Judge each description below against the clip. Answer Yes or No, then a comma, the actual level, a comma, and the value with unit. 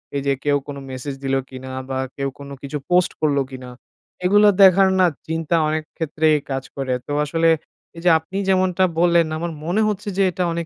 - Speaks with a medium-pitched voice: Yes, medium, 160 Hz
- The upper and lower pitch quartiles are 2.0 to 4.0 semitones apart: No, average, 4.4 semitones